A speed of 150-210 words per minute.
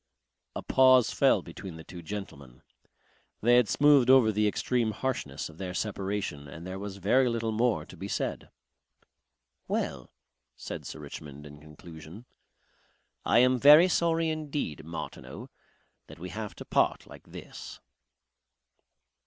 No: average, 140 wpm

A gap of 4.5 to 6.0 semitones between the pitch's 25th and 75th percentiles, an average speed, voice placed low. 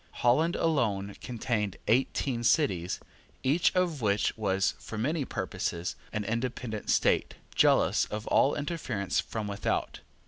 No: wide, 5.4 semitones; slow, 125 wpm; low, 115 Hz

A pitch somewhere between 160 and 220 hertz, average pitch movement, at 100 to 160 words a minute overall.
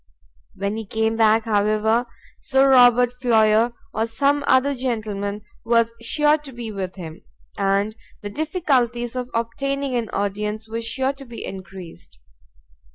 No: high, 230 Hz; average, 3.3 semitones; average, 140 wpm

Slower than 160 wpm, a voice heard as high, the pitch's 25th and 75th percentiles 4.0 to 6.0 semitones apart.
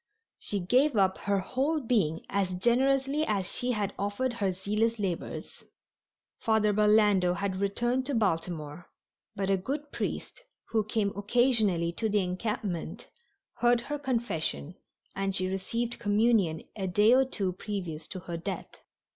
Yes: average, 145 wpm; high, 205 Hz; average, 4.3 semitones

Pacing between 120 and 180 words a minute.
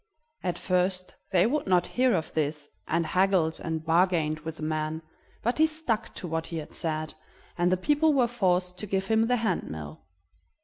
No: average, 190 wpm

